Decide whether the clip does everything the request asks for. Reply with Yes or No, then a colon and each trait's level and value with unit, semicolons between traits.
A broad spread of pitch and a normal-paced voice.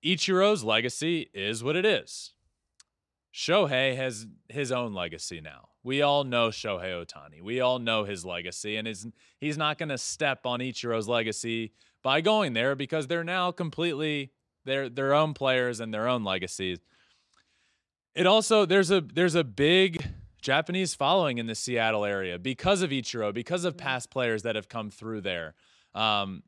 Yes: wide, 5.9 semitones; average, 165 wpm